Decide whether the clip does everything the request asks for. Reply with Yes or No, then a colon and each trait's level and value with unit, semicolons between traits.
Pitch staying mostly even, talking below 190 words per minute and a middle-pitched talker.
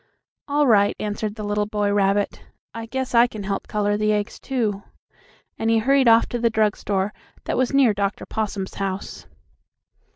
No: narrow, 2.2 semitones; average, 175 wpm; high, 210 Hz